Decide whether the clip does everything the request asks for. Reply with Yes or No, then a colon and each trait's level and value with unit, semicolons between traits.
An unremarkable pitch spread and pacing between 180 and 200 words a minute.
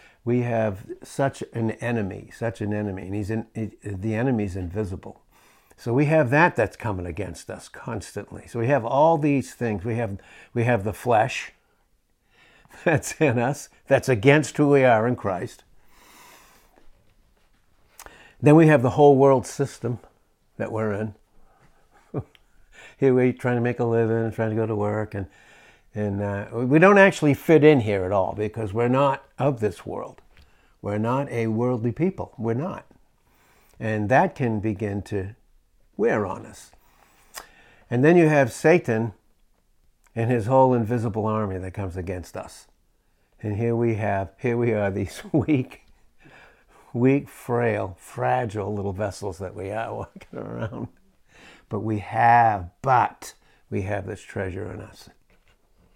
No: average, 3.6 semitones; average, 155 wpm